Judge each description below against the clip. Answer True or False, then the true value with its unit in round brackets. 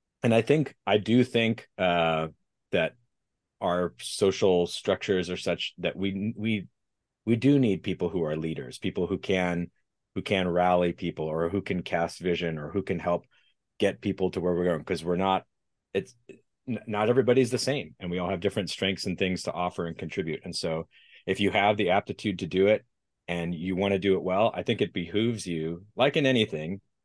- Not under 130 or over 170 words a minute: False (200 wpm)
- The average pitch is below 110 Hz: True (95 Hz)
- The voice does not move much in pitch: False (3.5 semitones)